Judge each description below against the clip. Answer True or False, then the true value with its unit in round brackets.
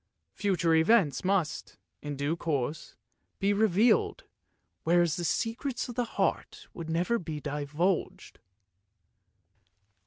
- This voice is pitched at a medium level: True (170 Hz)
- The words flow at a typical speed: False (105 wpm)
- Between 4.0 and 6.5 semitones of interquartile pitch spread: True (4.9 semitones)